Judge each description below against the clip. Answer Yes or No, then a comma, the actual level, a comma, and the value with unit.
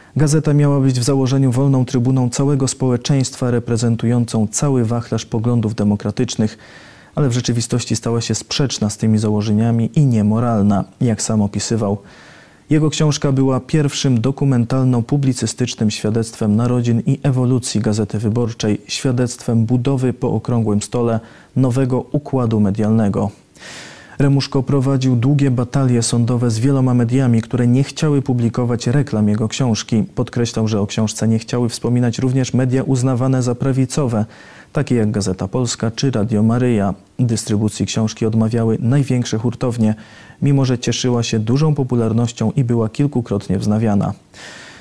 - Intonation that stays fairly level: No, average, 3.0 semitones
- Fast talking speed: No, average, 130 wpm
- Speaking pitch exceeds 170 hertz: No, low, 120 Hz